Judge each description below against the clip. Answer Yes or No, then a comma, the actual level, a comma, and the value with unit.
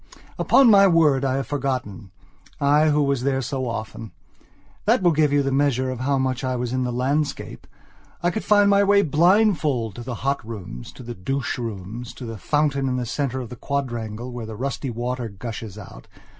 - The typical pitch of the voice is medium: No, low, 130 Hz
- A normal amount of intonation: Yes, average, 3.4 semitones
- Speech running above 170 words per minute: Yes, average, 200 wpm